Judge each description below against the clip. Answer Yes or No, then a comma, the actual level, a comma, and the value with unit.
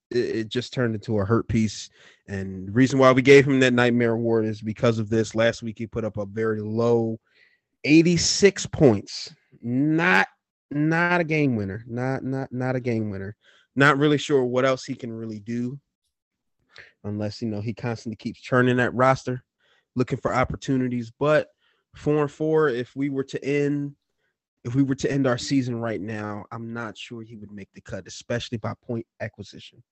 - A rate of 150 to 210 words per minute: Yes, average, 185 wpm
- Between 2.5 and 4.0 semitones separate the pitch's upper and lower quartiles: Yes, average, 3.4 semitones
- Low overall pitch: Yes, low, 120 Hz